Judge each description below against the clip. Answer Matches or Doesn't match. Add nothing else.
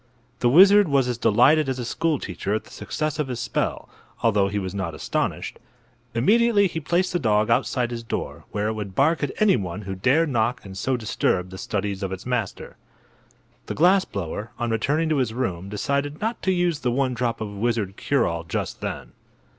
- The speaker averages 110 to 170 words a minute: Doesn't match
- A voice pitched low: Matches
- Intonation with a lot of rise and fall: Matches